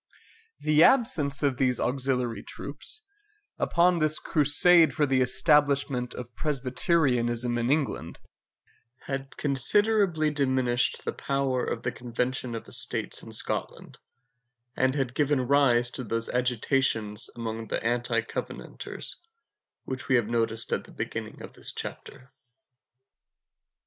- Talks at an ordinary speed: No, slow, 125 wpm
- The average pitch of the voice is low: Yes, low, 130 Hz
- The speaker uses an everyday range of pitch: Yes, average, 3.4 semitones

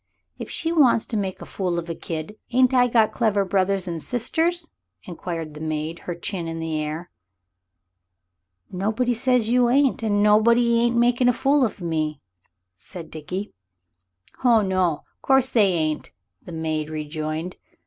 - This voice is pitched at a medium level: No, high, 195 Hz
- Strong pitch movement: Yes, wide, 6.7 semitones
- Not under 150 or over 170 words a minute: Yes, average, 160 wpm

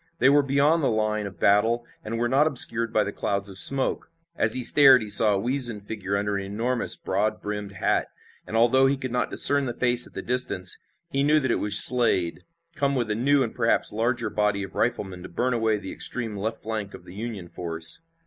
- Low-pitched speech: Yes, low, 115 Hz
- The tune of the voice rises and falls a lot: No, average, 3.7 semitones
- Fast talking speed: Yes, fast, 225 wpm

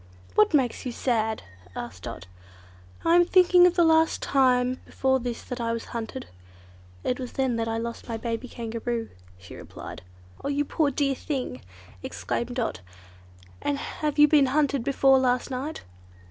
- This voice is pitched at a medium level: No, very high, 255 Hz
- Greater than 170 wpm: No, average, 160 wpm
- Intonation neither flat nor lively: Yes, average, 3.6 semitones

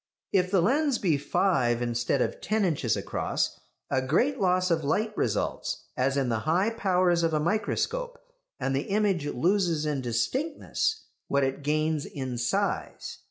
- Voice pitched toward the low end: No, medium, 165 Hz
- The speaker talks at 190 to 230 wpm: No, average, 160 wpm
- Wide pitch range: Yes, wide, 7.1 semitones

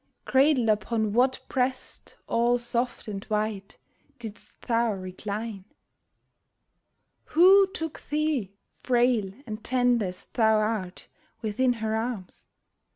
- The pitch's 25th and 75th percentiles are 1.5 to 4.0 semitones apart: Yes, average, 3.0 semitones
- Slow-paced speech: Yes, slow, 105 wpm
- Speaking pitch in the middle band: No, high, 230 Hz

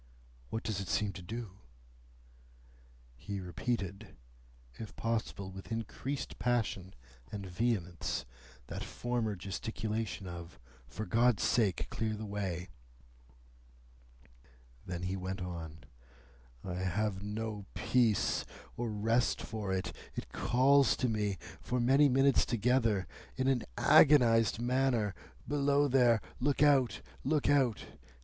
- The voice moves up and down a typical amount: Yes, average, 4.3 semitones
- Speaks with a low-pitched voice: Yes, low, 110 Hz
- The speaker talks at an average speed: No, slow, 115 wpm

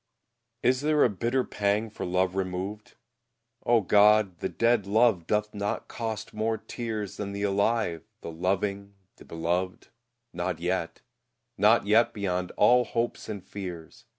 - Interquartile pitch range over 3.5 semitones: No, average, 3.2 semitones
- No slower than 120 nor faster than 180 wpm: Yes, average, 150 wpm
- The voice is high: No, low, 100 Hz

